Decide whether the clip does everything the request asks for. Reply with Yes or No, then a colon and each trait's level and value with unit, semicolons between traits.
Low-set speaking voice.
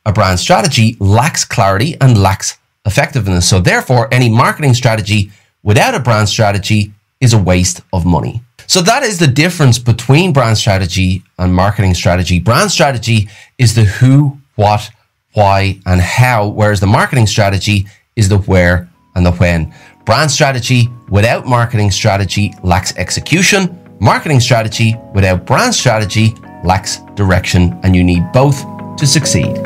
Yes: low, 110 Hz